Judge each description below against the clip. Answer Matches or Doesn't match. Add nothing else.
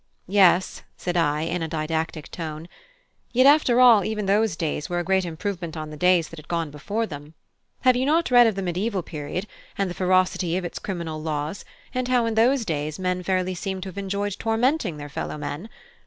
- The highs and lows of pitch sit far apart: Doesn't match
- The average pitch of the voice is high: Doesn't match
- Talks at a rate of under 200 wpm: Doesn't match